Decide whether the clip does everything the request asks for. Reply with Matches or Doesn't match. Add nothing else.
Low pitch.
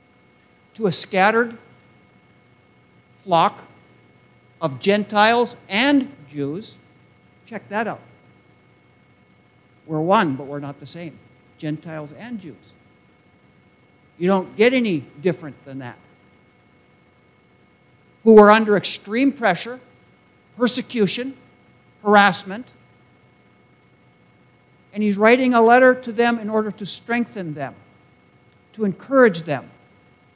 Doesn't match